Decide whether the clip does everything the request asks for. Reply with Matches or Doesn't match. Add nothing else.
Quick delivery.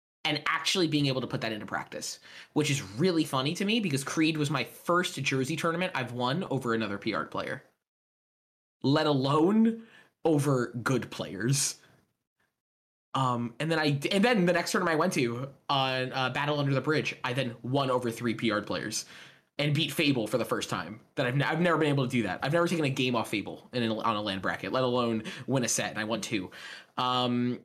Matches